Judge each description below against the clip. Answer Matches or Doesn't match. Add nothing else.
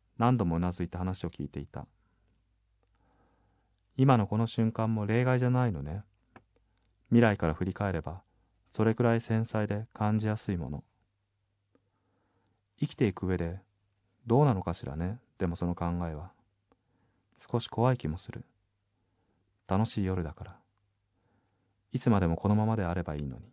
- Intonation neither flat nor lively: Matches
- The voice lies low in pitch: Matches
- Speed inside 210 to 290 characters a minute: Matches